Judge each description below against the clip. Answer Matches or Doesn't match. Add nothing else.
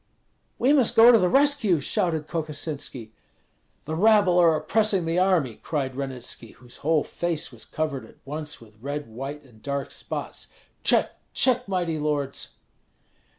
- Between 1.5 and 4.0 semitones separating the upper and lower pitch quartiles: Doesn't match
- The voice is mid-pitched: Matches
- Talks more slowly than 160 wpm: Matches